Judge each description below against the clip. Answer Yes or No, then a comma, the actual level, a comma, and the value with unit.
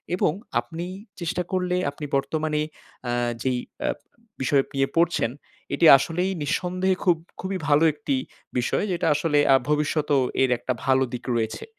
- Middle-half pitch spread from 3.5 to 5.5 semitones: Yes, average, 4.4 semitones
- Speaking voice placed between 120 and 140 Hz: No, medium, 150 Hz